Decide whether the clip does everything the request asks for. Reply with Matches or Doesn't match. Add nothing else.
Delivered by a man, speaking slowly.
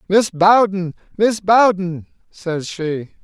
Matches